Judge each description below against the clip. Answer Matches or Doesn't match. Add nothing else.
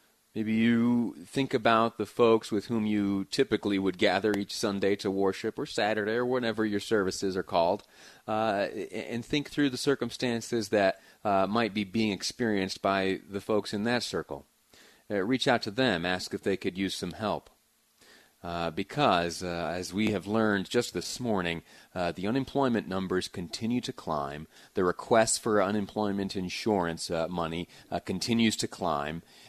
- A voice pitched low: Matches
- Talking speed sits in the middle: Matches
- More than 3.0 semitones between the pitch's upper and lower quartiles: Matches